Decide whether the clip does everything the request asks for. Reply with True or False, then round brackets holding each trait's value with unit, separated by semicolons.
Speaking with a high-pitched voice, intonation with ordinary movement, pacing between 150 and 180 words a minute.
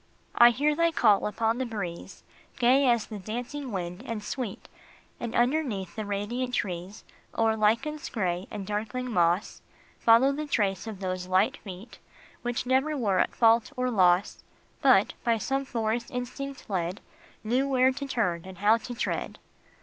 True (225 Hz; 4.3 semitones; 170 wpm)